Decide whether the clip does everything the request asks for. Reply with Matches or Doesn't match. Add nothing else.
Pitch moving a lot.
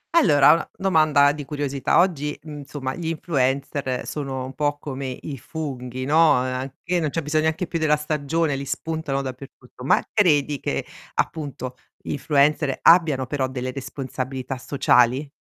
Doesn't match